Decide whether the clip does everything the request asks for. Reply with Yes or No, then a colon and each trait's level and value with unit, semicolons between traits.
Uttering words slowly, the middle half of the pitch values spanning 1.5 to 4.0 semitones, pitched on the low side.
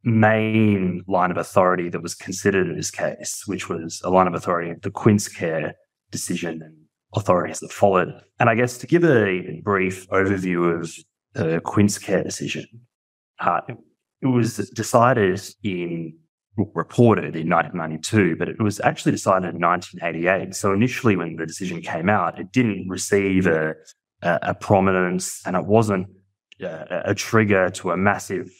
No: average, 155 wpm; average, 3.5 semitones; very low, 95 Hz